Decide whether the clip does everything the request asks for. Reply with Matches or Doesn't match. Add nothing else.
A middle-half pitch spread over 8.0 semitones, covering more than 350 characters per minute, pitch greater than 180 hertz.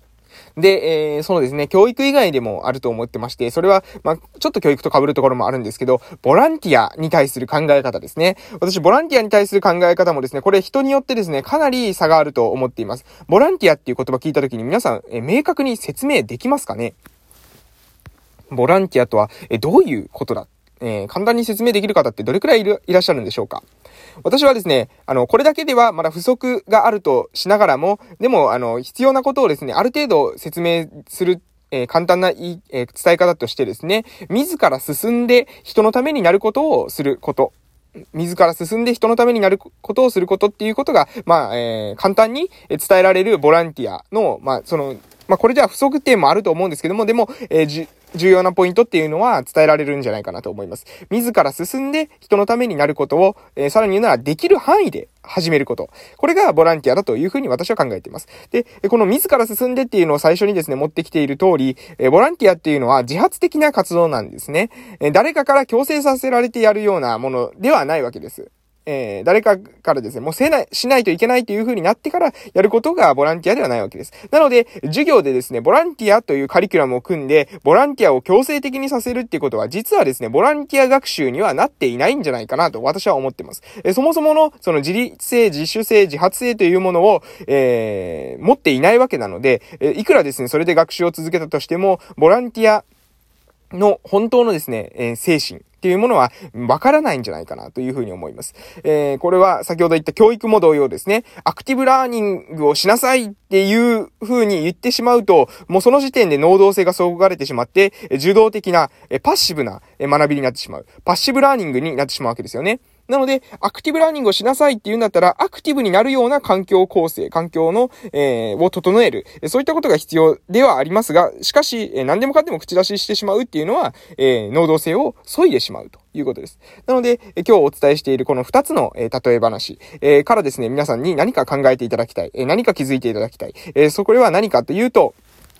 Matches